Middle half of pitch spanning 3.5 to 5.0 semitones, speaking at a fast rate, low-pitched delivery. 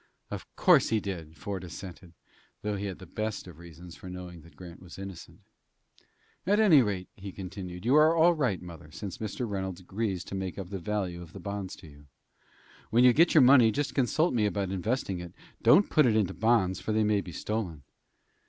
Yes: average, 3.9 semitones; fast, 210 wpm; very low, 95 Hz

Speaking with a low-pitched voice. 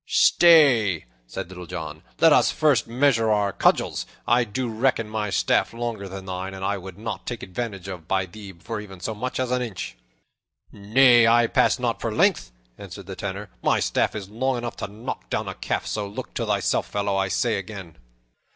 Yes: low, 105 Hz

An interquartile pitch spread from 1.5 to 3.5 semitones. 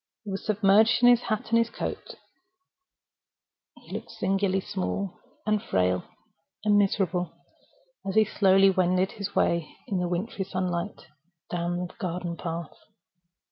Yes: average, 2.7 semitones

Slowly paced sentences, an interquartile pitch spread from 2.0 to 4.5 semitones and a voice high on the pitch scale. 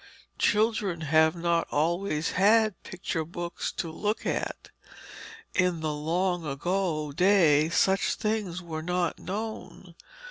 No: slow, 115 wpm; average, 3.5 semitones; medium, 175 Hz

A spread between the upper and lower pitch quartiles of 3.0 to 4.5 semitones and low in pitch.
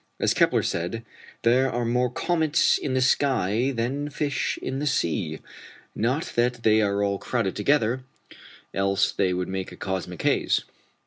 No: average, 5.1 semitones; low, 115 Hz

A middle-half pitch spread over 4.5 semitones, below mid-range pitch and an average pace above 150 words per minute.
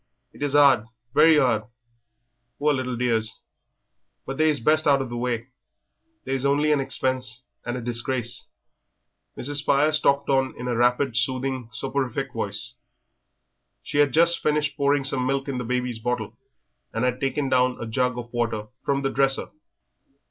No: narrow, 2.5 semitones; low, 130 Hz; average, 165 wpm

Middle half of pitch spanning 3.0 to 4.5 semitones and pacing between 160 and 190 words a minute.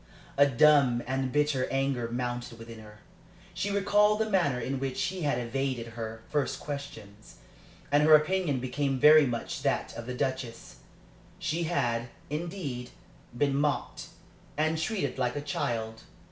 No: average, 4.0 semitones; average, 145 wpm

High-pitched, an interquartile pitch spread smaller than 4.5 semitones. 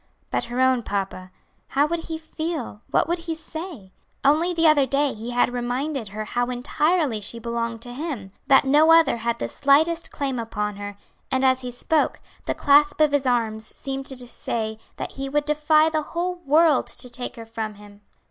No: very high, 265 Hz; average, 4.9 semitones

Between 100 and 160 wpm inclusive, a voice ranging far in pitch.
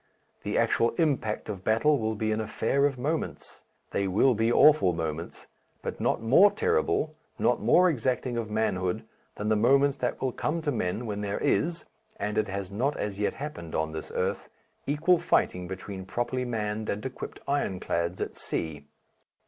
No: average, 175 wpm; wide, 6.0 semitones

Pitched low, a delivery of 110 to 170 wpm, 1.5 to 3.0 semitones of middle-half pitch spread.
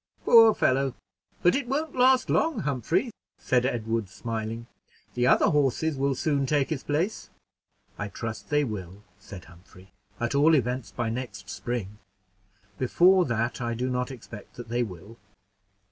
No: low, 125 Hz; average, 150 wpm; average, 4.8 semitones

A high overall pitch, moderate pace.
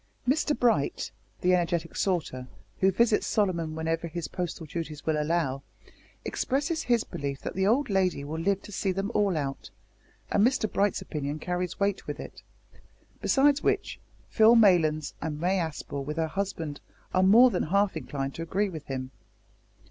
No: medium, 175 Hz; average, 165 wpm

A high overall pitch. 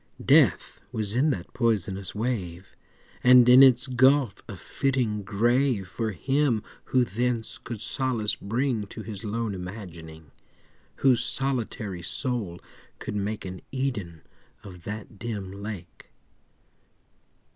No: low, 110 Hz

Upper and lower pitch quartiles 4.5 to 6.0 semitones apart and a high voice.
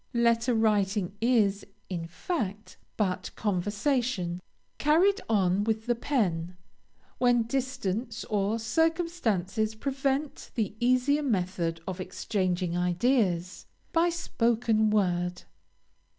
Yes: average, 5.3 semitones; high, 220 Hz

